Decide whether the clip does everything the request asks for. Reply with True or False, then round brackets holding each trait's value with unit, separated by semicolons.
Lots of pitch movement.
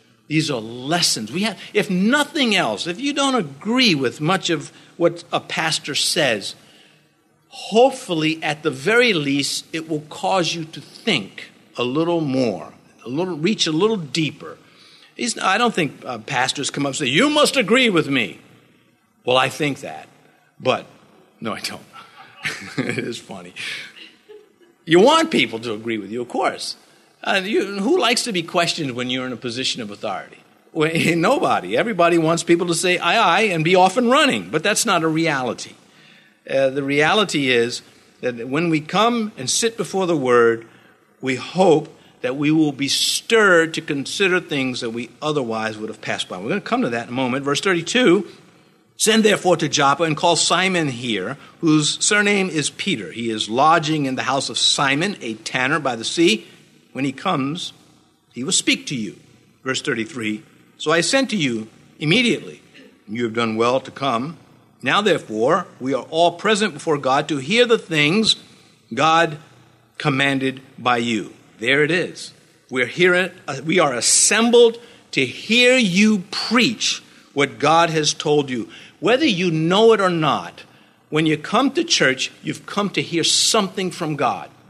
True (5.9 semitones)